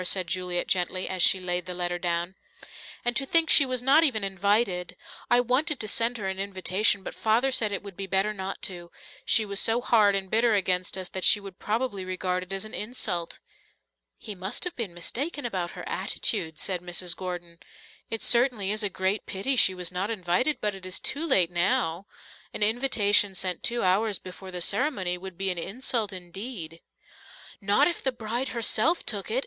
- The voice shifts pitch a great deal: No, average, 4.1 semitones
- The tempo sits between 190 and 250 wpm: Yes, average, 195 wpm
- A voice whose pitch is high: Yes, high, 195 Hz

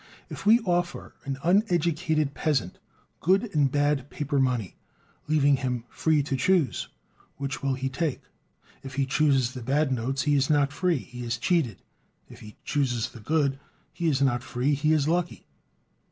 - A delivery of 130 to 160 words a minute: No, average, 170 wpm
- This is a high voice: No, medium, 140 Hz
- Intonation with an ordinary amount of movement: Yes, average, 3.2 semitones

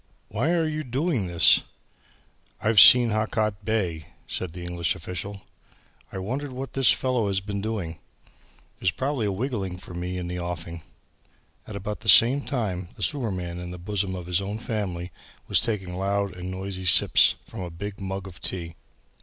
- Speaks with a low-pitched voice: Yes, very low, 95 Hz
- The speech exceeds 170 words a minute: Yes, average, 180 wpm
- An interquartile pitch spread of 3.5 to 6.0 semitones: Yes, average, 3.8 semitones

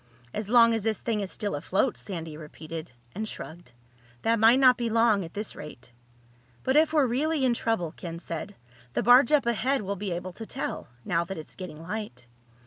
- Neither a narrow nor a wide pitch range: No, wide, 5.9 semitones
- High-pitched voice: Yes, high, 210 Hz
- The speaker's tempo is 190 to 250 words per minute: Yes, average, 195 wpm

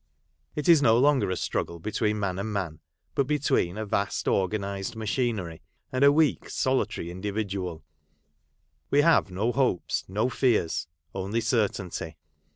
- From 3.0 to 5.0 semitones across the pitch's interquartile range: No, wide, 5.6 semitones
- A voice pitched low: Yes, low, 105 Hz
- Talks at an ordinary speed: Yes, average, 145 wpm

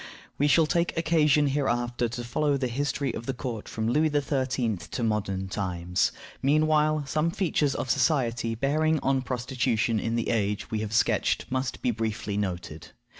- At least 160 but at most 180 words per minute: Yes, average, 165 wpm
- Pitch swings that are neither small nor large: Yes, average, 4.7 semitones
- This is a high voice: No, low, 125 Hz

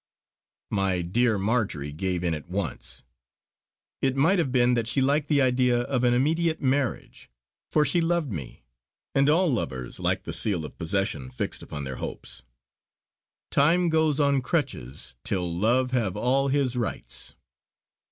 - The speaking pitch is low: Yes, low, 125 Hz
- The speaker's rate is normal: Yes, average, 150 wpm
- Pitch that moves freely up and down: Yes, wide, 7.4 semitones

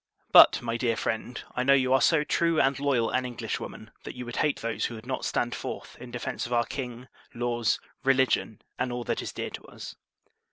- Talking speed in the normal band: No, fast, 215 wpm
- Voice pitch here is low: Yes, low, 125 Hz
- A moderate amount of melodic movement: No, narrow, 1.9 semitones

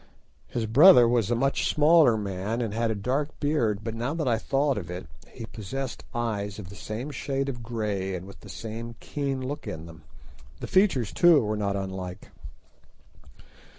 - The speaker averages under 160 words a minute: No, average, 185 wpm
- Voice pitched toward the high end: No, low, 115 Hz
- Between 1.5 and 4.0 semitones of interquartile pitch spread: No, average, 5.1 semitones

